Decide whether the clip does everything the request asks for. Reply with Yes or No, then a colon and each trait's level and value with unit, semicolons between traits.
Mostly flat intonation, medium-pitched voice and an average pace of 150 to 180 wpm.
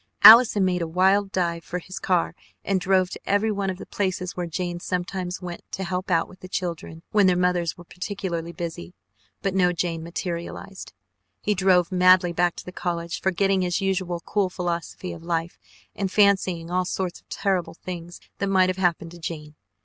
No: narrow, 1.8 semitones; medium, 180 Hz; average, 190 wpm